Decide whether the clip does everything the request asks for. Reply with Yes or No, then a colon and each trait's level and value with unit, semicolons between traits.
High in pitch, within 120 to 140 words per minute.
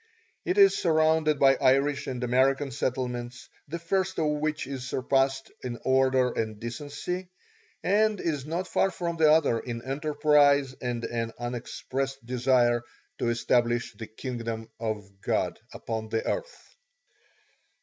No: low, 135 Hz; slow, 135 wpm